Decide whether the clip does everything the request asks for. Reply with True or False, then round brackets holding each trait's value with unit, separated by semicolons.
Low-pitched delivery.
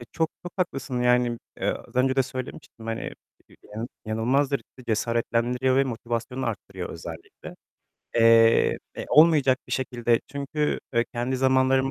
True (125 Hz)